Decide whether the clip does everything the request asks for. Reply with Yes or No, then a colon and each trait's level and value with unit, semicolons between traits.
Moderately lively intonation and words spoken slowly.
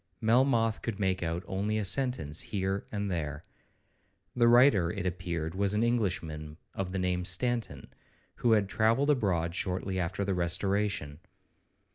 No: average, 3.9 semitones; average, 150 wpm